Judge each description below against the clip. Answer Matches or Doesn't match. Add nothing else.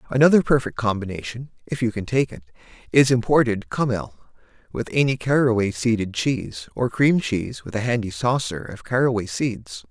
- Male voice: Matches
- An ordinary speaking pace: Matches